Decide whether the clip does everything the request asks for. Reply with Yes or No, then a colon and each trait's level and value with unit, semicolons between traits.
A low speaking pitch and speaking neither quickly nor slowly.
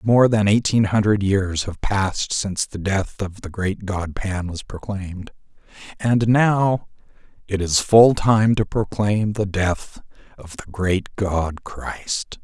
Yes: low, 100 Hz; average, 155 wpm